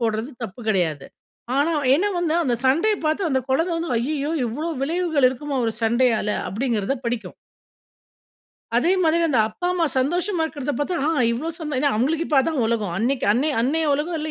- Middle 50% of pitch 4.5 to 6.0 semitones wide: Yes, average, 5.3 semitones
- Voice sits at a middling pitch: No, very high, 285 Hz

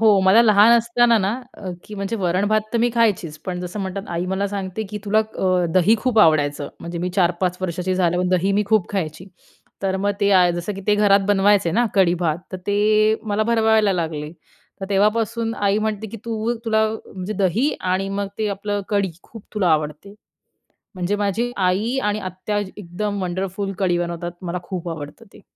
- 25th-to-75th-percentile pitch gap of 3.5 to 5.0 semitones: No, average, 2.9 semitones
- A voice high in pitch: Yes, high, 195 Hz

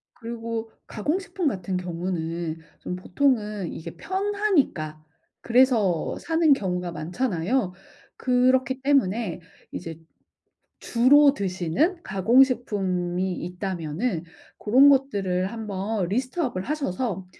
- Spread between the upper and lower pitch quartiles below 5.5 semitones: No, wide, 6.5 semitones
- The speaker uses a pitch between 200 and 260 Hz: Yes, high, 210 Hz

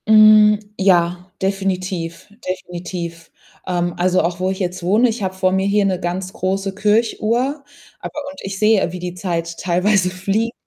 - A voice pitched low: No, medium, 185 Hz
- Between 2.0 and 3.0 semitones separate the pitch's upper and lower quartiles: Yes, average, 2.7 semitones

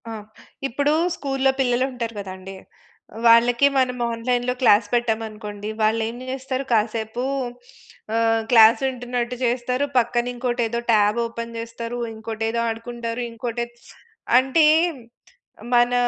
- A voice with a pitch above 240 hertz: No, high, 235 Hz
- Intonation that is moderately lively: No, narrow, 1.7 semitones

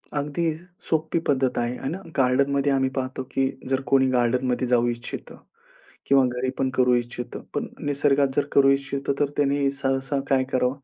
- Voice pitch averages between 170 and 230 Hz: No, low, 135 Hz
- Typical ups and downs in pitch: No, narrow, 1.7 semitones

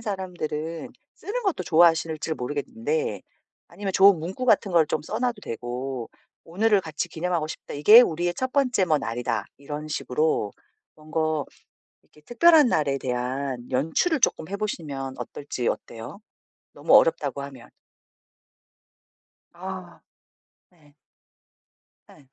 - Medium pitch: Yes, medium, 160 Hz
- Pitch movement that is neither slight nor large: No, wide, 5.9 semitones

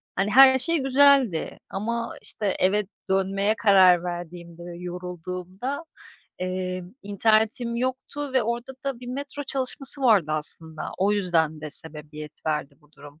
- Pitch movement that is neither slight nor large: No, wide, 6.3 semitones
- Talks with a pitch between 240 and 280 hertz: No, high, 195 Hz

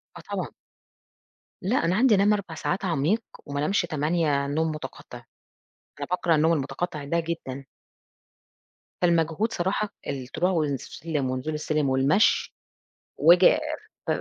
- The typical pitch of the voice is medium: Yes, medium, 160 Hz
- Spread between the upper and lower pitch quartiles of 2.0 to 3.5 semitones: No, average, 4.0 semitones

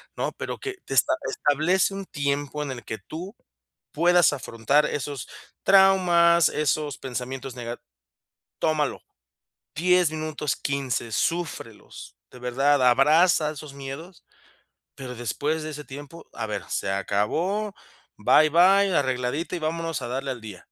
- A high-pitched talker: No, medium, 150 Hz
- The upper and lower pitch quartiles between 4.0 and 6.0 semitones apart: Yes, average, 4.5 semitones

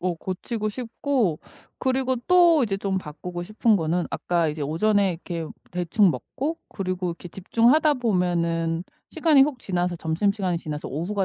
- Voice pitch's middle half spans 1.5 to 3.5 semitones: No, wide, 5.5 semitones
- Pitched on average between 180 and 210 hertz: Yes, medium, 185 Hz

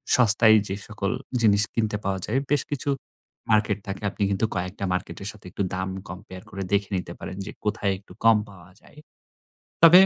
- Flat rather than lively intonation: Yes, narrow, 2.3 semitones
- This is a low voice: Yes, low, 100 Hz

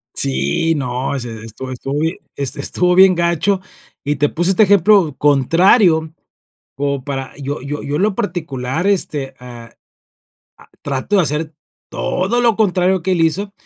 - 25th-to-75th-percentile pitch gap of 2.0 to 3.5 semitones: No, wide, 5.4 semitones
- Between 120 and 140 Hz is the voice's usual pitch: No, medium, 160 Hz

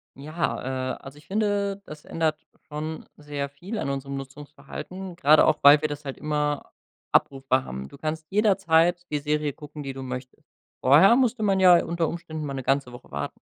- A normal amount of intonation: Yes, average, 3.8 semitones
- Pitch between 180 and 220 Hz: No, medium, 150 Hz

